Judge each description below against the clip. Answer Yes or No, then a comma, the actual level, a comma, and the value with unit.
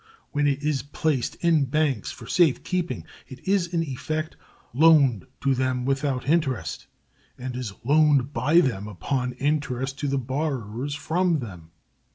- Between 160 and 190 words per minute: No, average, 150 wpm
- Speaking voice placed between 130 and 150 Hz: Yes, medium, 140 Hz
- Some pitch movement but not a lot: Yes, average, 3.5 semitones